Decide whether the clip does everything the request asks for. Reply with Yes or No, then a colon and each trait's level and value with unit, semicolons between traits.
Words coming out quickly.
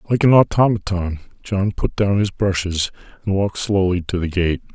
No: average, 175 wpm